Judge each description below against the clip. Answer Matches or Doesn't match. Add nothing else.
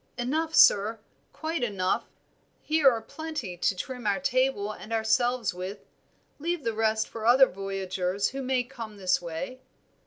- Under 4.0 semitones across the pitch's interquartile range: Doesn't match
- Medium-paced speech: Matches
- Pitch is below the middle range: Doesn't match